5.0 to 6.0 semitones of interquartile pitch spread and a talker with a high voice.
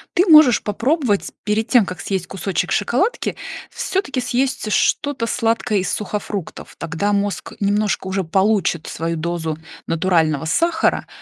Yes: wide, 5.4 semitones; high, 205 Hz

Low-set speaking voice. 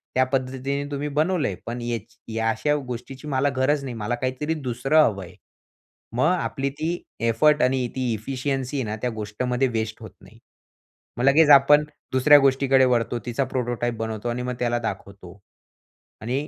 Yes: low, 130 Hz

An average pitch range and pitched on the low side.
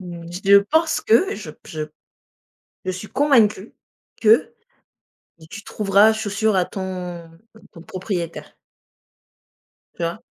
No: average, 3.7 semitones; high, 200 Hz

